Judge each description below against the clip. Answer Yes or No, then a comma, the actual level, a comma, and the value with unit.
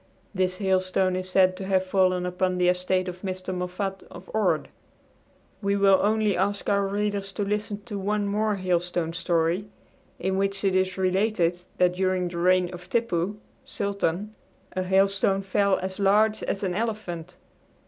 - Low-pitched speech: No, high, 190 Hz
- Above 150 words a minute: Yes, average, 160 wpm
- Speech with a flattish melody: Yes, narrow, 1.7 semitones